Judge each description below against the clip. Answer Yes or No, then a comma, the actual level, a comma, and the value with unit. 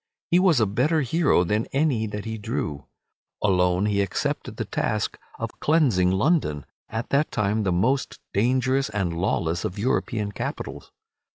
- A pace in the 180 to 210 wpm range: No, average, 155 wpm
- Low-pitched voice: Yes, low, 105 Hz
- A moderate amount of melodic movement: No, wide, 5.9 semitones